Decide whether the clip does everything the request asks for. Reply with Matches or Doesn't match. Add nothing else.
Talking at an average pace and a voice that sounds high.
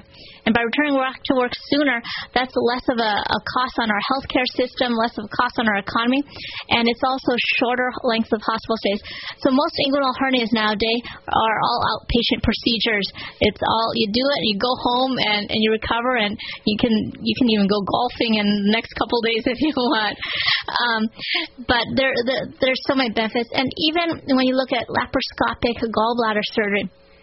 Matches